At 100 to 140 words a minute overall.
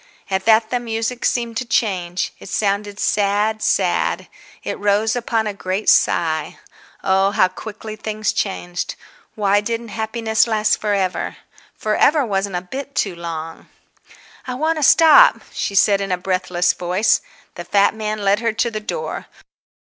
No: average, 160 wpm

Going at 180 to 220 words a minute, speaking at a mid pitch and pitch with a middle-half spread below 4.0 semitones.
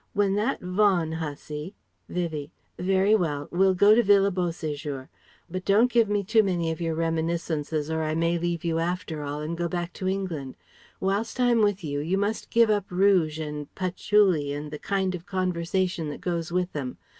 Yes: average, 190 wpm; medium, 175 Hz; average, 3.5 semitones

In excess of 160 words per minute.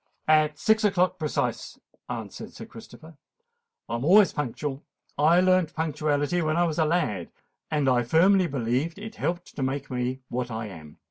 Yes: average, 170 wpm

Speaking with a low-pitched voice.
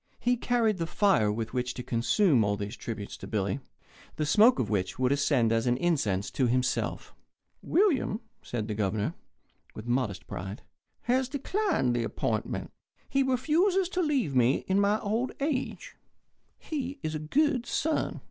No: medium, 155 Hz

